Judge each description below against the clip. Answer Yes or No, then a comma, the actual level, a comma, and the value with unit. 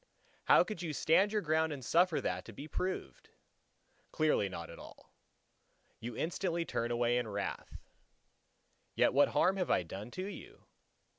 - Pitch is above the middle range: No, medium, 150 Hz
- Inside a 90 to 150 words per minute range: No, average, 160 wpm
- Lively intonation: Yes, wide, 7.3 semitones